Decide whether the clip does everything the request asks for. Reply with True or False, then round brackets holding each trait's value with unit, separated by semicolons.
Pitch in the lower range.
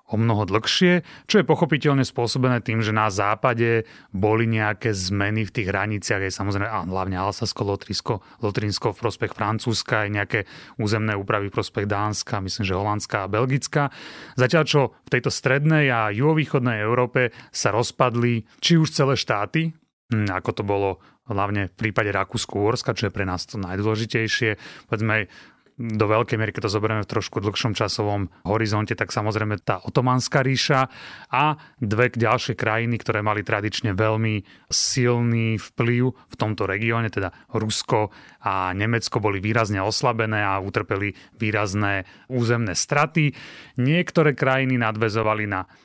True (110 Hz)